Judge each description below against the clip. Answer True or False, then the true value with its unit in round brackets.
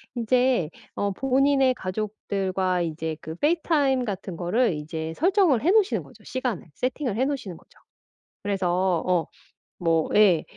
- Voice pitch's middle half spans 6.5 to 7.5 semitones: True (6.8 semitones)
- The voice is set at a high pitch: True (205 Hz)